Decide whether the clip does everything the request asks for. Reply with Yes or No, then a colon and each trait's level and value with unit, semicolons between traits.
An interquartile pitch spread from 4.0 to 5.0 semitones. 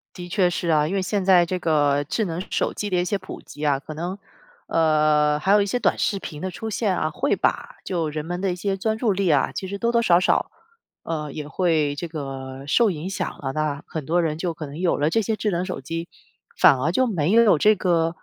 Yes: average, 4.3 semitones